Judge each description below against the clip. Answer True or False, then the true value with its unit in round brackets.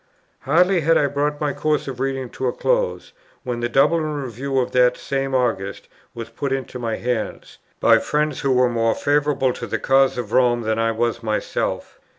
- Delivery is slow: False (190 wpm)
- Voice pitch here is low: True (130 Hz)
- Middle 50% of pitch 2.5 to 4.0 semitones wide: True (3.2 semitones)